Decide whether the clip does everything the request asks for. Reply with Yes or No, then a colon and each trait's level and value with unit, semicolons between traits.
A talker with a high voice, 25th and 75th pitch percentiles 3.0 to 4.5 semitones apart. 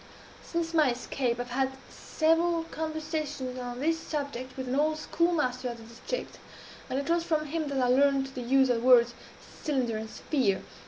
Yes: very high, 270 Hz; average, 4.0 semitones